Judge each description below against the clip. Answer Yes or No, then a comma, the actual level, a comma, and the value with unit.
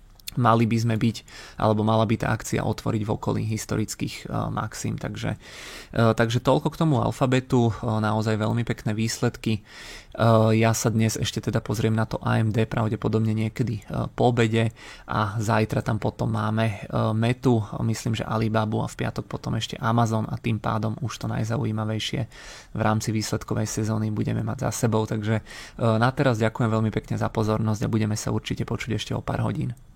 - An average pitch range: No, narrow, 1.4 semitones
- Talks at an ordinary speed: No, fast, 180 wpm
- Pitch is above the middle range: No, low, 110 Hz